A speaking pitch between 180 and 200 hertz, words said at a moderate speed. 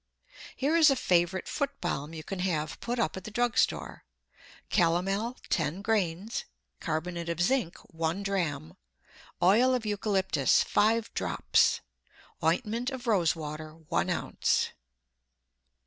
No: high, 190 Hz; slow, 130 wpm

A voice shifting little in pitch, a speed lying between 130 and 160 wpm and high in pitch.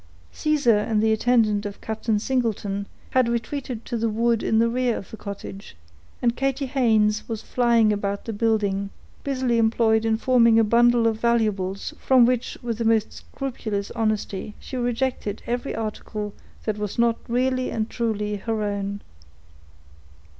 Yes: narrow, 2.3 semitones; average, 155 wpm; high, 225 Hz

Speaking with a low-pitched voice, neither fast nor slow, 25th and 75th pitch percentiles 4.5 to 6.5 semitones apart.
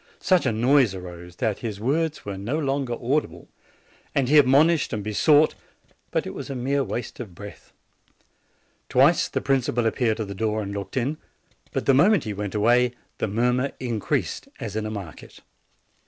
Yes: low, 120 Hz; average, 180 wpm; average, 4.8 semitones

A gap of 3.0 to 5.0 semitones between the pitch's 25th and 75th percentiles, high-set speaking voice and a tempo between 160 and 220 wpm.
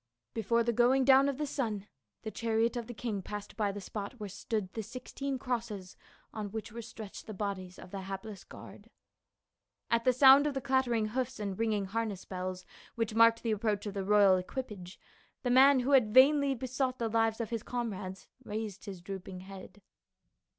Yes: average, 3.7 semitones; high, 220 Hz; average, 190 wpm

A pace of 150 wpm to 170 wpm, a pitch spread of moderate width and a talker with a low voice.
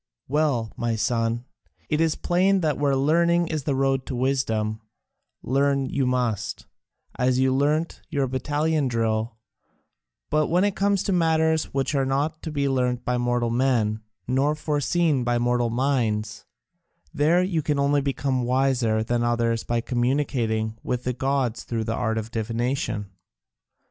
Yes: average, 155 wpm; average, 3.9 semitones; low, 130 Hz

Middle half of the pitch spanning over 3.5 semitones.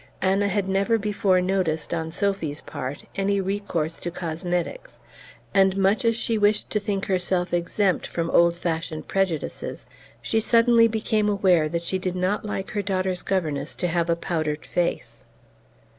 No: average, 3.0 semitones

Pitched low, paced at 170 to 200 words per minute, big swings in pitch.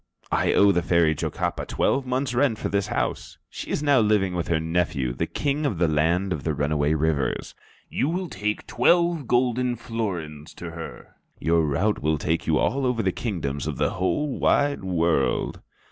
Yes: very low, 90 Hz; average, 185 wpm; wide, 7.8 semitones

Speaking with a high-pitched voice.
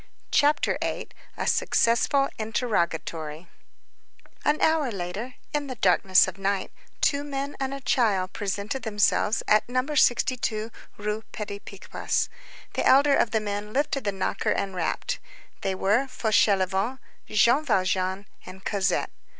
Yes: high, 215 Hz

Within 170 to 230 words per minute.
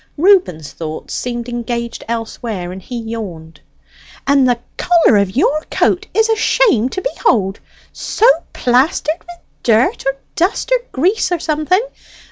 No: average, 140 wpm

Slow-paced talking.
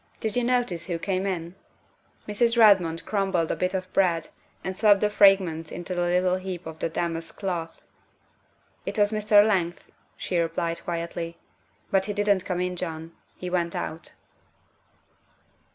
No: average, 165 wpm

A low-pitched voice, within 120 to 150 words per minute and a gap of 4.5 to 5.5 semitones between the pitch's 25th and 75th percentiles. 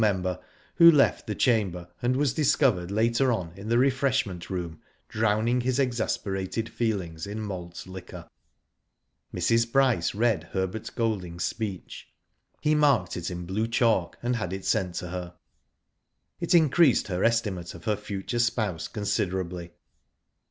Yes: low, 105 Hz; average, 140 wpm; average, 4.8 semitones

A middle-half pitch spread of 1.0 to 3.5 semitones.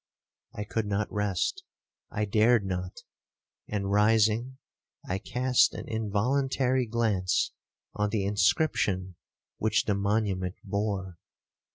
Yes: narrow, 2.4 semitones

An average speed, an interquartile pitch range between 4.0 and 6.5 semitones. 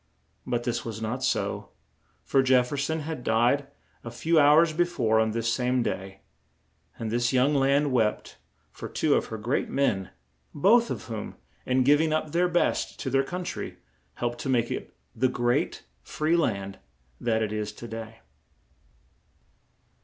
Yes: average, 170 wpm; average, 4.5 semitones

